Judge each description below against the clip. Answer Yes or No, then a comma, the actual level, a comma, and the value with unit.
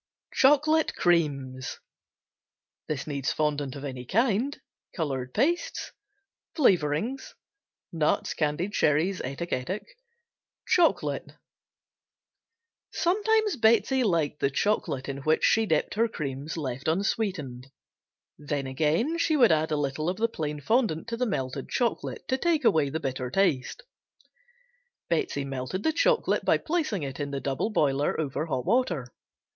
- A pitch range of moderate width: No, wide, 8.8 semitones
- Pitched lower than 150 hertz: No, medium, 160 Hz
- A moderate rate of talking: No, slow, 130 wpm